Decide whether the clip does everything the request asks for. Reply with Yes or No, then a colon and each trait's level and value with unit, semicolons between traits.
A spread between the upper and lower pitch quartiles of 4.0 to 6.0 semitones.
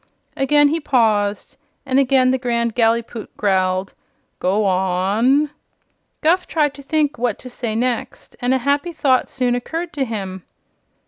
Yes: average, 4.8 semitones